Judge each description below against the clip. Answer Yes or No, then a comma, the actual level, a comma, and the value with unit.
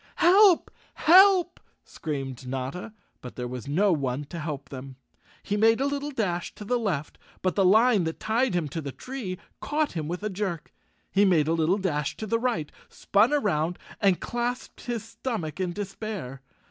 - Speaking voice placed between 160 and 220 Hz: Yes, high, 190 Hz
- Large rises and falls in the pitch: Yes, wide, 7.2 semitones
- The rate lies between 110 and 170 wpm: No, average, 180 wpm